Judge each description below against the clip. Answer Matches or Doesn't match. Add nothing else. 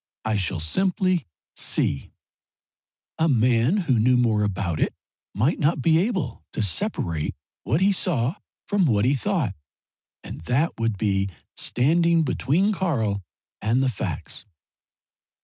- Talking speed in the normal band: Doesn't match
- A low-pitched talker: Matches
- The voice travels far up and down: Matches